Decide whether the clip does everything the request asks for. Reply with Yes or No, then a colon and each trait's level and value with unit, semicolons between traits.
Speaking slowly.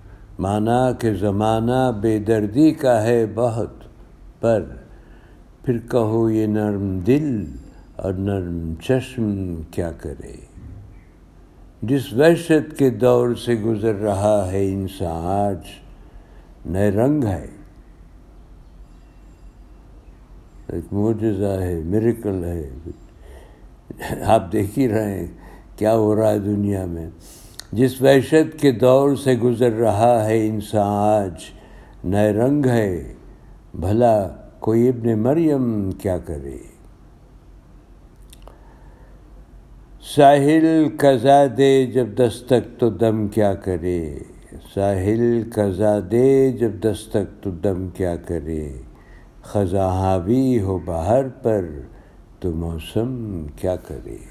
Yes: slow, 105 wpm